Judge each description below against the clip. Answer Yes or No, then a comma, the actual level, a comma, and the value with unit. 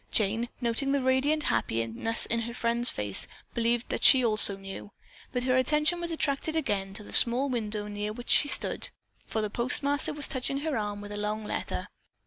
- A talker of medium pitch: No, high, 235 Hz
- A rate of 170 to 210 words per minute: Yes, average, 190 wpm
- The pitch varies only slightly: No, average, 4.7 semitones